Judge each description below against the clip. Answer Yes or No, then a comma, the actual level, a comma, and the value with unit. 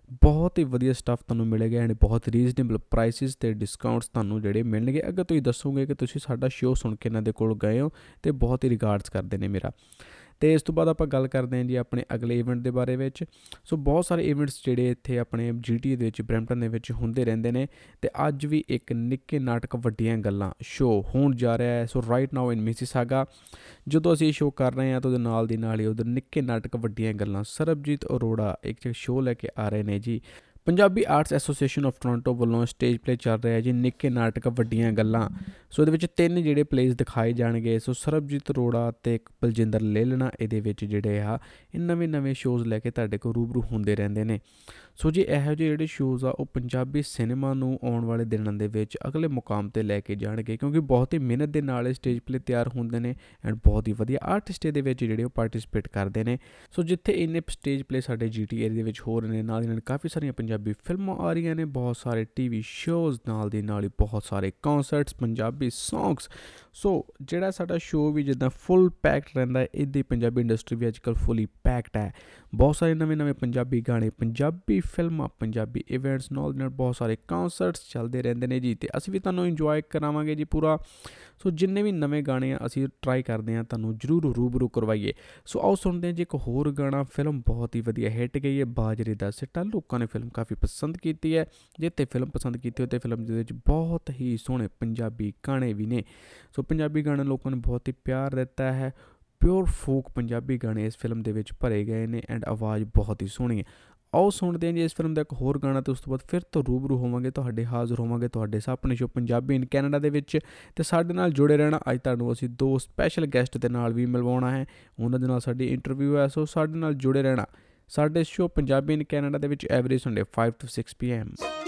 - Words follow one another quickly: Yes, fast, 215 wpm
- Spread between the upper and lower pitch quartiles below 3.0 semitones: No, average, 4.0 semitones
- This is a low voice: Yes, low, 125 Hz